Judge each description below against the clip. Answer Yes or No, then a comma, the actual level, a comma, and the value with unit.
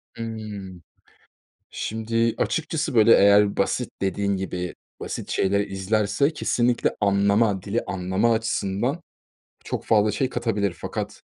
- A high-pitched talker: No, low, 105 Hz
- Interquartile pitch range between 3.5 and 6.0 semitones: No, average, 2.8 semitones